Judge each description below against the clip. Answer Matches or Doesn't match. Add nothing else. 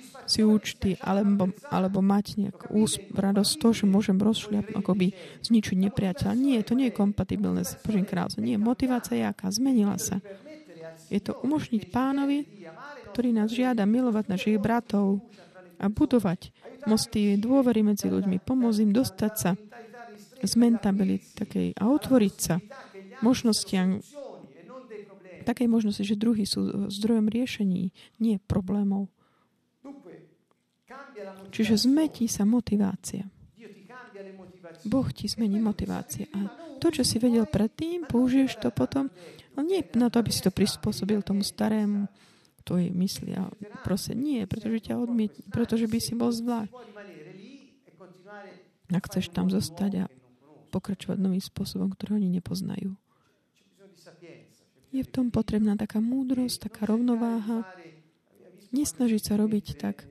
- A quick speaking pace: Doesn't match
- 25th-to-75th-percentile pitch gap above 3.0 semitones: Matches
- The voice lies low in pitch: Doesn't match